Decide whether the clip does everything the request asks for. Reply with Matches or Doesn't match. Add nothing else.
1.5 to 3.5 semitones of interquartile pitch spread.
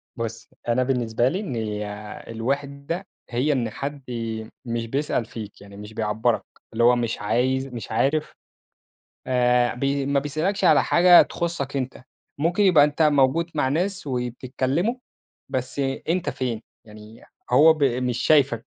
Doesn't match